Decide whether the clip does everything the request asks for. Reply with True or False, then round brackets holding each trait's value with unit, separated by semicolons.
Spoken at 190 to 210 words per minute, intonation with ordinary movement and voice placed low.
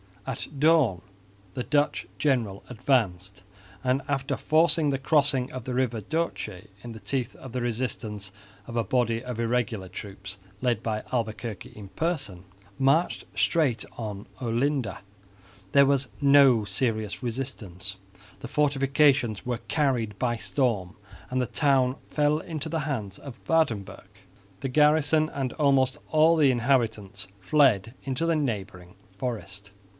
False (135 wpm; 4.6 semitones; 125 Hz)